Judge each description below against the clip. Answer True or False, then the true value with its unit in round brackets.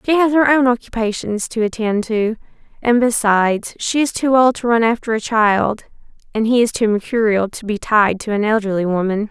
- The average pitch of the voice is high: True (225 Hz)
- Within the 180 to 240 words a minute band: True (200 wpm)